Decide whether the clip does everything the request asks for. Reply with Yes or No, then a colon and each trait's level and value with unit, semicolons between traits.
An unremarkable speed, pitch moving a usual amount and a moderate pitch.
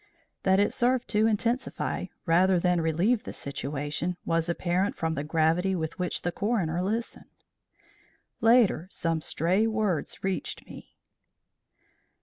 No: slow, 130 wpm; average, 4.3 semitones; medium, 180 Hz